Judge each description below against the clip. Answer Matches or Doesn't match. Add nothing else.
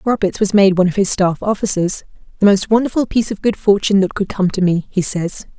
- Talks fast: Matches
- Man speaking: Doesn't match